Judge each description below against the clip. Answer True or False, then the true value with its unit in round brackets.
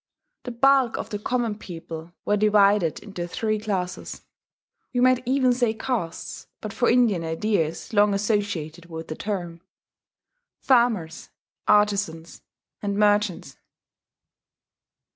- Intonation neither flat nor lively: True (4.6 semitones)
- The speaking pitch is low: False (205 Hz)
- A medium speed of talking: False (115 wpm)